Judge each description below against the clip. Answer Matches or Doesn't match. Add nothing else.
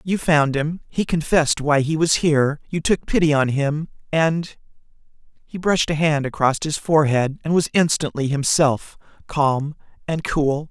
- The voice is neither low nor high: Matches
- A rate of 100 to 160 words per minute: Matches